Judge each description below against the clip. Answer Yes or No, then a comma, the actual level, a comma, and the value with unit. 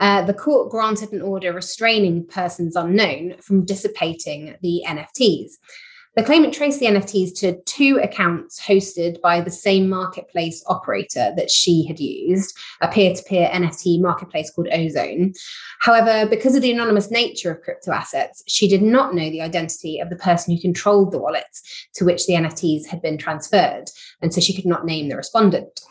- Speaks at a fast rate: No, average, 175 wpm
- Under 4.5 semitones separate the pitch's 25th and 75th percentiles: Yes, average, 3.3 semitones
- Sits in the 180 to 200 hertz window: Yes, medium, 185 Hz